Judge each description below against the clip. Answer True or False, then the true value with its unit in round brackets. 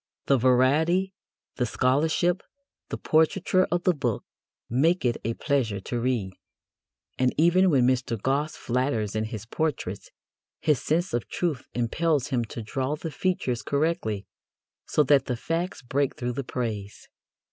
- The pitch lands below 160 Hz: True (135 Hz)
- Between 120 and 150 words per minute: True (145 wpm)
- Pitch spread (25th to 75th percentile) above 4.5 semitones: True (5.1 semitones)